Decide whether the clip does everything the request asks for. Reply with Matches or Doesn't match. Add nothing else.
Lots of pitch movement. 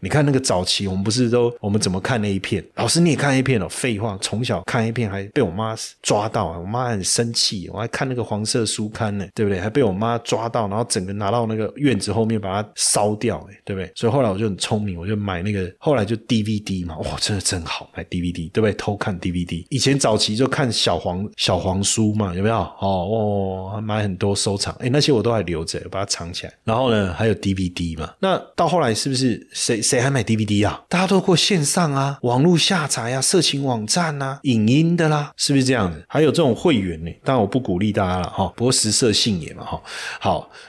Doesn't match